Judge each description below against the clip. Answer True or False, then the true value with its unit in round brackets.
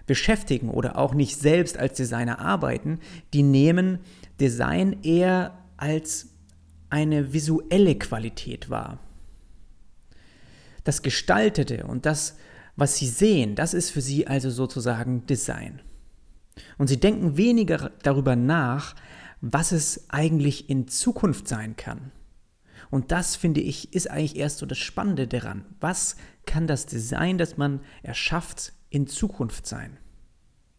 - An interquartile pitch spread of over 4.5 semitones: True (5.2 semitones)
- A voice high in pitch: False (140 Hz)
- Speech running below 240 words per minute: True (125 wpm)